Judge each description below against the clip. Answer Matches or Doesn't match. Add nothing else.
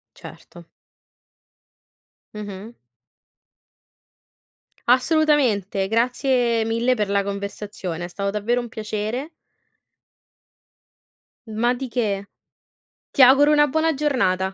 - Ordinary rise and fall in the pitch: Matches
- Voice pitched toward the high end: Matches